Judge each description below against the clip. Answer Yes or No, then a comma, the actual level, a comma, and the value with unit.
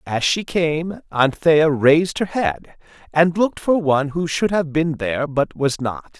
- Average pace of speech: Yes, average, 185 wpm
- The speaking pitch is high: No, medium, 155 Hz